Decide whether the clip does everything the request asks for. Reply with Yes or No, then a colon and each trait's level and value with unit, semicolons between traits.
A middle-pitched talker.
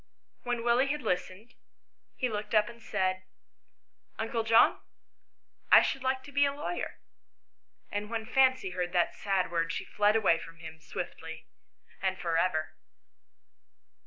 No: high, 210 Hz